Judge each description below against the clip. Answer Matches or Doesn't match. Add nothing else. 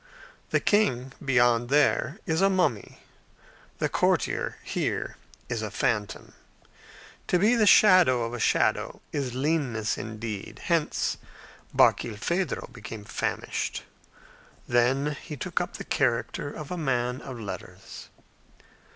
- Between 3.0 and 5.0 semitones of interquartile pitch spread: Doesn't match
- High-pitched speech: Doesn't match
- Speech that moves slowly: Matches